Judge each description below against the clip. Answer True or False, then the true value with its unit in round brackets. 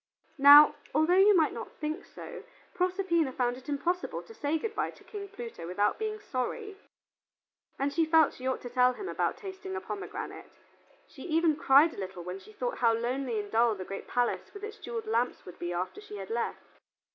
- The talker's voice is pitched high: True (280 Hz)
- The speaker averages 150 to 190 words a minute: False (205 wpm)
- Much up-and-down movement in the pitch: True (7.9 semitones)